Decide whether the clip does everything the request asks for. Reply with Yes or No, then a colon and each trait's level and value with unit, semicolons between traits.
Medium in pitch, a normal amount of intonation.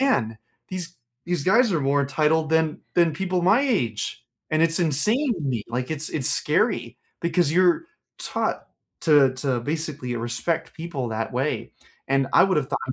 Yes: medium, 155 Hz; average, 4.7 semitones